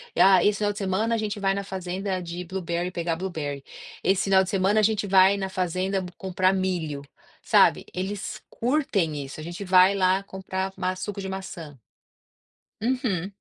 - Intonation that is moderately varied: No, narrow, 1.7 semitones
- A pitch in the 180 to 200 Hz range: Yes, high, 190 Hz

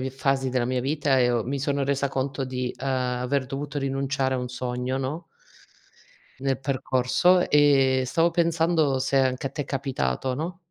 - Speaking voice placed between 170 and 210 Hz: No, low, 135 Hz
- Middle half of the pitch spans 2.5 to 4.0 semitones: No, narrow, 1.7 semitones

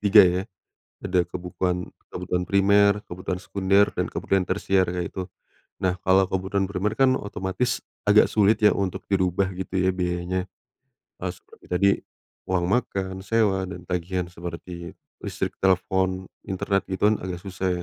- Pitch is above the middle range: No, very low, 95 Hz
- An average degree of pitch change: No, narrow, 1.5 semitones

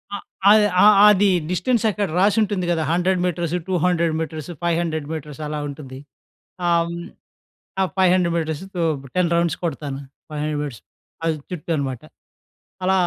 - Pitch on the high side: No, medium, 170 Hz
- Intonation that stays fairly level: No, average, 3.1 semitones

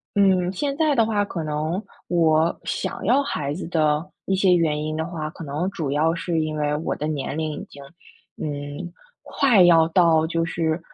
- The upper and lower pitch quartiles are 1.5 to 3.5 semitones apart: Yes, average, 3.0 semitones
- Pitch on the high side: No, medium, 165 Hz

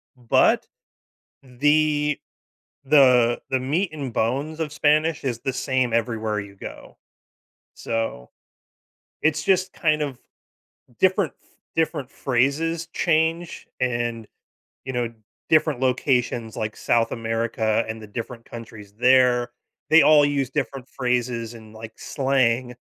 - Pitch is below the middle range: Yes, low, 130 Hz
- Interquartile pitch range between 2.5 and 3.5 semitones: No, average, 4.4 semitones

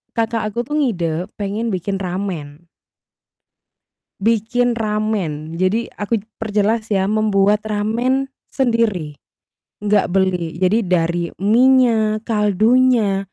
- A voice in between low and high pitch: No, high, 210 Hz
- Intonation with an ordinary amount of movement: Yes, average, 3.5 semitones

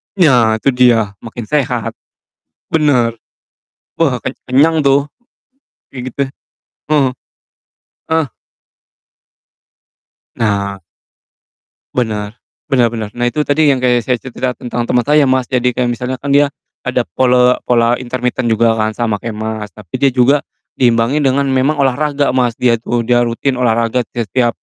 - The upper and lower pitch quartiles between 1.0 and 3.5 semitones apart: Yes, average, 2.7 semitones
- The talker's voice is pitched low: Yes, low, 125 Hz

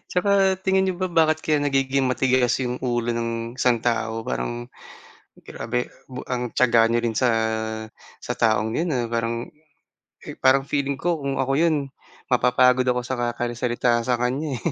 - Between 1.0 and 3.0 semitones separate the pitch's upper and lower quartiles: Yes, narrow, 2.6 semitones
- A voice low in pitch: Yes, low, 125 Hz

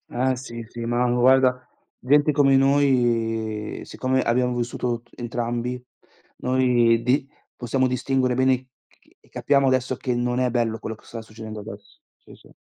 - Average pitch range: No, narrow, 1.8 semitones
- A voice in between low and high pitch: No, low, 125 Hz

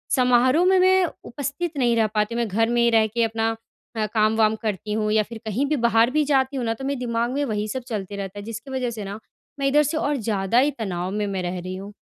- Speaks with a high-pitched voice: Yes, high, 225 Hz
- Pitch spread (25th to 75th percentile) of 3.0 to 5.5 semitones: Yes, average, 3.7 semitones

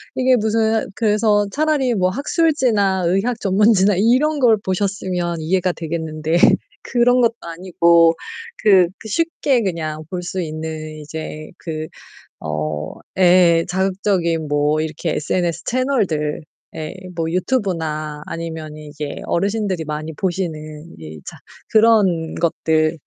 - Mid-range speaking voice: Yes, medium, 175 Hz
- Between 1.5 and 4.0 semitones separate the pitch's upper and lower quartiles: No, average, 5.2 semitones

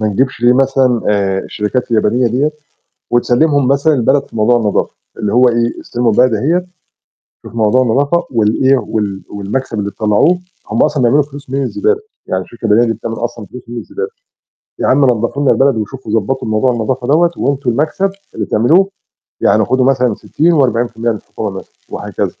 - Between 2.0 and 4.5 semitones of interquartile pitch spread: Yes, average, 3.7 semitones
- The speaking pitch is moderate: No, low, 125 Hz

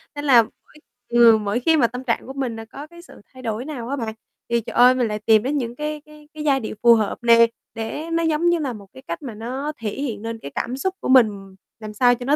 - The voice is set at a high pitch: Yes, high, 245 Hz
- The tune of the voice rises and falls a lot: No, average, 4.3 semitones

